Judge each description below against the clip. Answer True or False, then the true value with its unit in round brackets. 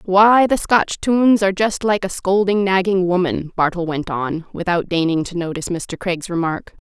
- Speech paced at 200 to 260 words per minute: False (185 wpm)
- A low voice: False (185 Hz)